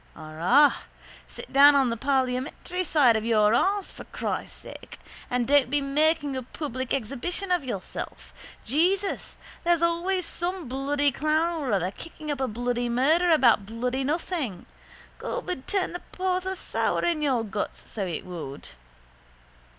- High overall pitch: Yes, very high, 280 Hz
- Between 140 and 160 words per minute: Yes, average, 150 wpm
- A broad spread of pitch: Yes, wide, 6.0 semitones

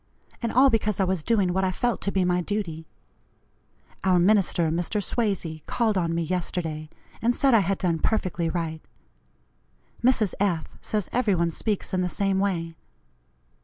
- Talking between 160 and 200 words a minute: Yes, average, 165 wpm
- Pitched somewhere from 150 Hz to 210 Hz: Yes, medium, 185 Hz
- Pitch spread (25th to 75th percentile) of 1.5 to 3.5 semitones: No, average, 3.9 semitones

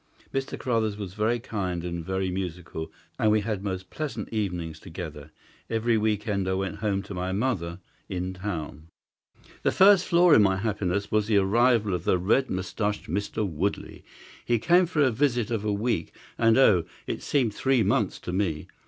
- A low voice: Yes, low, 100 Hz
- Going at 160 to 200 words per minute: Yes, average, 180 wpm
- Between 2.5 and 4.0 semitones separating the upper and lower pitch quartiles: Yes, average, 3.7 semitones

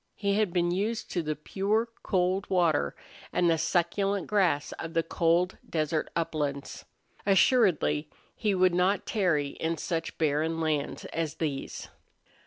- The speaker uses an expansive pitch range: No, average, 3.5 semitones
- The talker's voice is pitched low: No, medium, 170 Hz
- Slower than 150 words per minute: Yes, average, 140 wpm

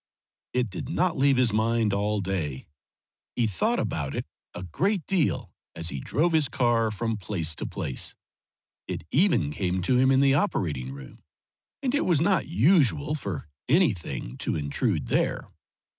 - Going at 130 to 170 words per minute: Yes, average, 160 wpm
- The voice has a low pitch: Yes, low, 115 Hz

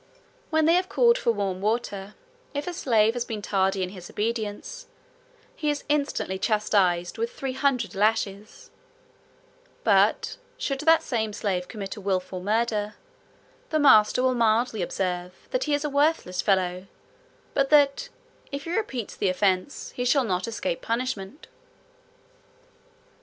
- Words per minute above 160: No, average, 145 wpm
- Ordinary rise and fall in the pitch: No, wide, 6.5 semitones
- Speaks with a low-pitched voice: No, high, 220 Hz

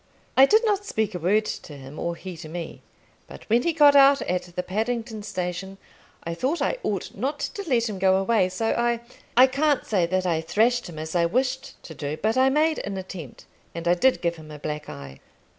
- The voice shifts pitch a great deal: Yes, wide, 7.2 semitones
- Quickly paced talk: Yes, fast, 225 wpm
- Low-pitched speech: No, high, 195 Hz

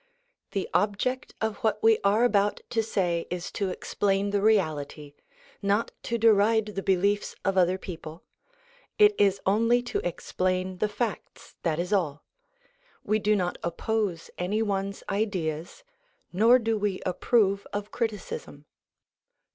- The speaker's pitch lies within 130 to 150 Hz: No, high, 200 Hz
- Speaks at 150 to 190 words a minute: No, average, 140 wpm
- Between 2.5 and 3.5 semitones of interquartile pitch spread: Yes, average, 3.0 semitones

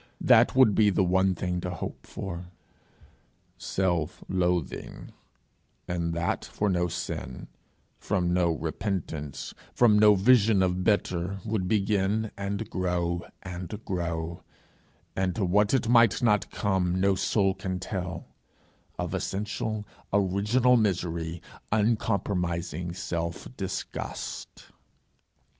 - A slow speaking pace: Yes, slow, 115 wpm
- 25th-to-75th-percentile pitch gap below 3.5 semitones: Yes, average, 2.9 semitones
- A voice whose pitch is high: No, very low, 95 Hz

